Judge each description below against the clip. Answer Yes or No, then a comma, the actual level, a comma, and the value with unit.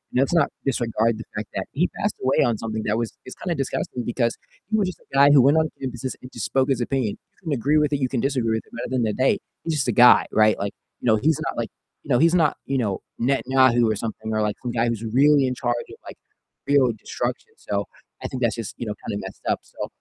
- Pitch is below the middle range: Yes, low, 125 Hz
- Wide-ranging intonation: No, average, 3.5 semitones